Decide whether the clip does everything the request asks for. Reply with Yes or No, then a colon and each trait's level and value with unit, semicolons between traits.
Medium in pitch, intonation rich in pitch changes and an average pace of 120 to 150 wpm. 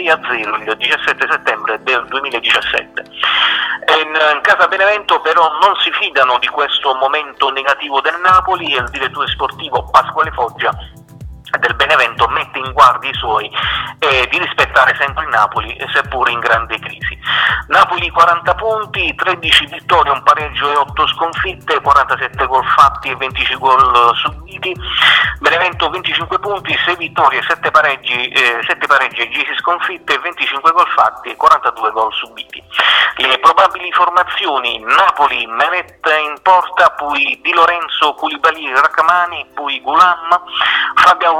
No: medium, 165 Hz; average, 3.8 semitones; average, 140 wpm